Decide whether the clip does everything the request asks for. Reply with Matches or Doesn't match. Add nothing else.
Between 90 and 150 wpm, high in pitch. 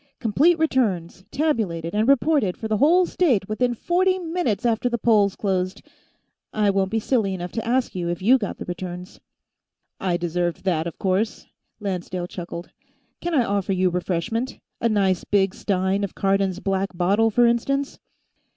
Doesn't match